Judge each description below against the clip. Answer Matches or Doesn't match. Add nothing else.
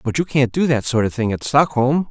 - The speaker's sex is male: Matches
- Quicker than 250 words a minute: Matches